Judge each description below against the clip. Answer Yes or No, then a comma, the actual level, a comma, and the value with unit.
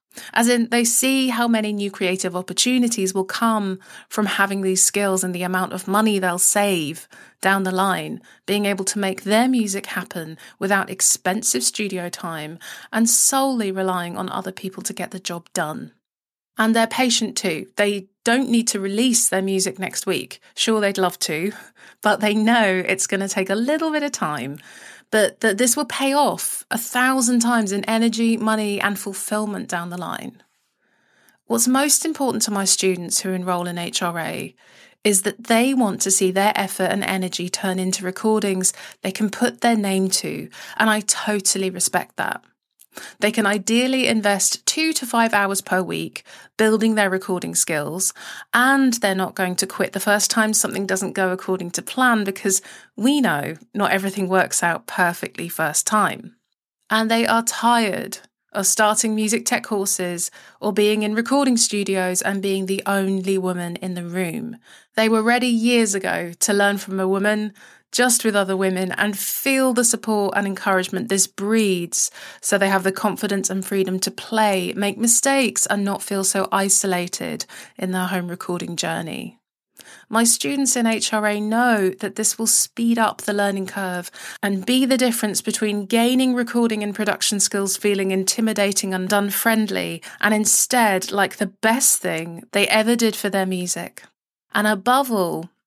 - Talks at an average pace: Yes, average, 170 wpm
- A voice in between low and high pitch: No, high, 200 Hz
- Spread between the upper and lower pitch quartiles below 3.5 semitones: Yes, average, 3.0 semitones